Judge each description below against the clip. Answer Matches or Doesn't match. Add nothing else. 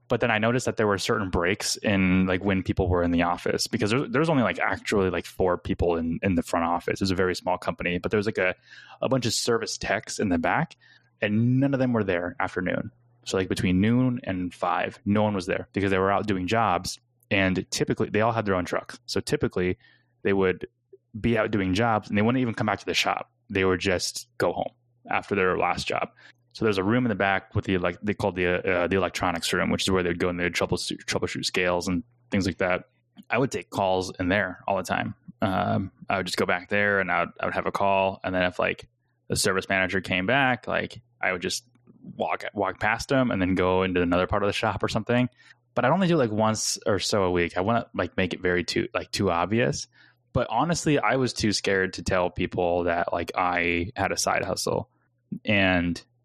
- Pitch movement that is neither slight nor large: Matches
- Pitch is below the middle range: Matches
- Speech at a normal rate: Doesn't match